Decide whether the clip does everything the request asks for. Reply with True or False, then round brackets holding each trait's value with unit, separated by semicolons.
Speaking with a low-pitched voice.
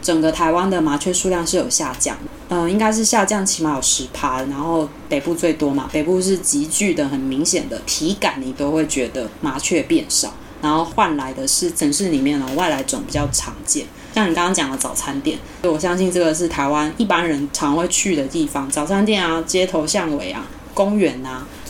False (170 Hz)